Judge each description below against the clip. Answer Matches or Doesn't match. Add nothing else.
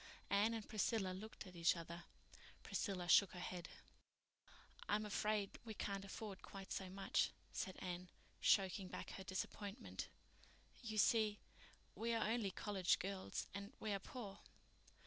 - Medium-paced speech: Matches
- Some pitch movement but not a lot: Doesn't match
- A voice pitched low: Doesn't match